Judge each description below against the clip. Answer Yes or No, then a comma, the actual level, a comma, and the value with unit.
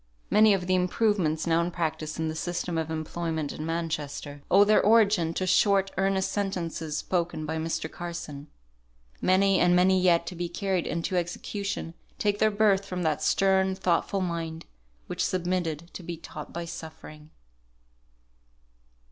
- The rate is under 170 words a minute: Yes, average, 155 wpm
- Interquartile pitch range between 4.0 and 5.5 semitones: No, average, 2.9 semitones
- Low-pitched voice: No, medium, 175 Hz